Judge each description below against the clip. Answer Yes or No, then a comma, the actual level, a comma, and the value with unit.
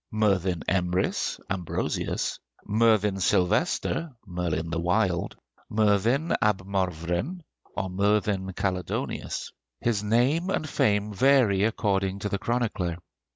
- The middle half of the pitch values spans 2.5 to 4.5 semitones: Yes, average, 3.3 semitones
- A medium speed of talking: No, slow, 105 wpm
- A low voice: Yes, low, 100 Hz